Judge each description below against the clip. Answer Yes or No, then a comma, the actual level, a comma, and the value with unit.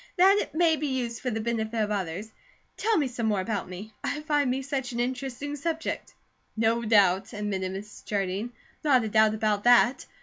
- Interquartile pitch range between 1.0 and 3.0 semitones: No, average, 4.4 semitones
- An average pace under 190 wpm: No, average, 195 wpm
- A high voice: Yes, high, 230 Hz